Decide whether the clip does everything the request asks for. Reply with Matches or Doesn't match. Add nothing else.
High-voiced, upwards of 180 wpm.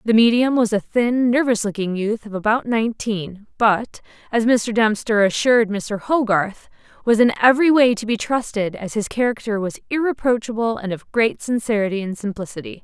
Doesn't match